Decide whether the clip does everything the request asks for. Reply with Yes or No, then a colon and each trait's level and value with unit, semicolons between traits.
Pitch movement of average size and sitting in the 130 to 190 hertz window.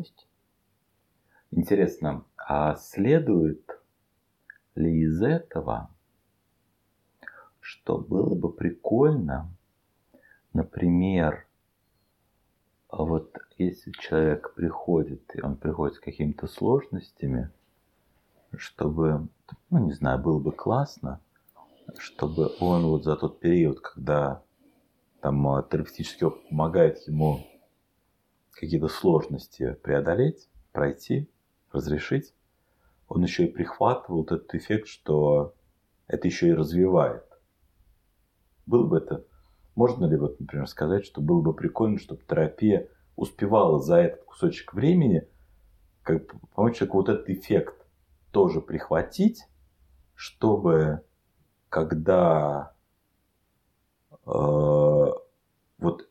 No: average, 4.7 semitones; very low, 80 Hz